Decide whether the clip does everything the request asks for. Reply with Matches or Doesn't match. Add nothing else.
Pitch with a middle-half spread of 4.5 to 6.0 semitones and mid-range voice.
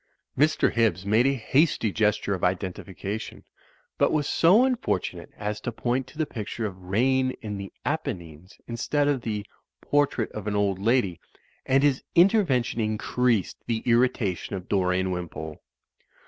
Doesn't match